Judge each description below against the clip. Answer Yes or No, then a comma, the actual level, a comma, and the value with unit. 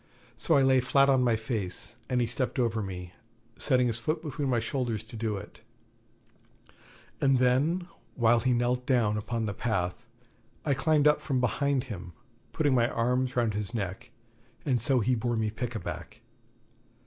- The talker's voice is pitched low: Yes, low, 120 Hz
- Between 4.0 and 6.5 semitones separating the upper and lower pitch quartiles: No, average, 2.9 semitones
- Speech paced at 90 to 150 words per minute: No, average, 170 wpm